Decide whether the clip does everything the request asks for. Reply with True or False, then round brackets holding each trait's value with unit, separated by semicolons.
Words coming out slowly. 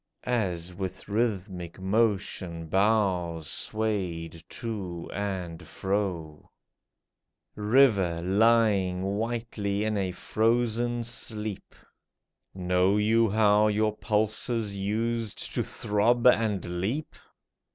True (90 wpm)